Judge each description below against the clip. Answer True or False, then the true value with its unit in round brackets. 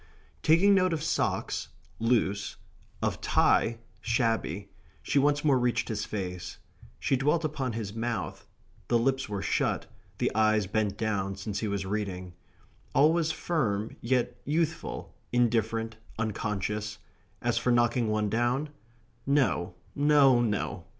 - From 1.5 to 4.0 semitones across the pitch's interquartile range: False (4.6 semitones)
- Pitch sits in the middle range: False (115 Hz)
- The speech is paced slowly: True (130 wpm)